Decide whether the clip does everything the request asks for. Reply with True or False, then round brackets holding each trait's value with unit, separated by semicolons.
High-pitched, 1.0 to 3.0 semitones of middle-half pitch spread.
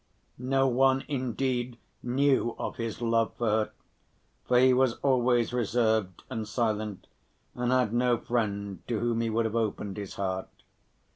False (120 Hz; 2.5 semitones)